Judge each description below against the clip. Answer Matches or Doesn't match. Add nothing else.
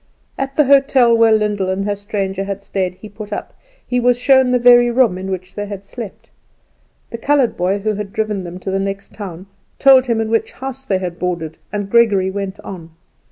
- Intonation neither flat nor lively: Matches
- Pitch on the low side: Doesn't match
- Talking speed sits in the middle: Doesn't match